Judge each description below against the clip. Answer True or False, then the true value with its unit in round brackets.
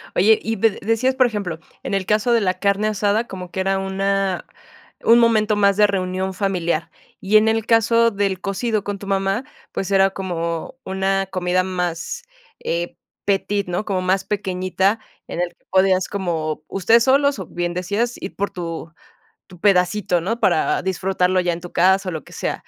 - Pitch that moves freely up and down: False (2.4 semitones)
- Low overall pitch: False (195 Hz)